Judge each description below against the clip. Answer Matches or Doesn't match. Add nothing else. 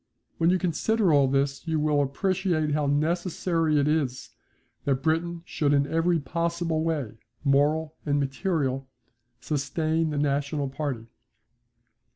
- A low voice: Doesn't match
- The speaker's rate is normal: Doesn't match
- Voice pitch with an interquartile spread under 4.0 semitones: Matches